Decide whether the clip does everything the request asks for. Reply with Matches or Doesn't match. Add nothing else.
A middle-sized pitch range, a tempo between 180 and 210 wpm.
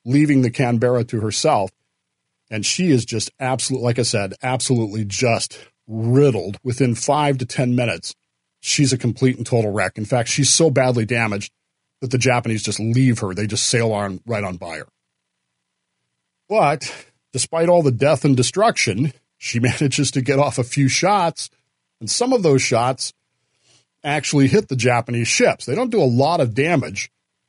Doesn't match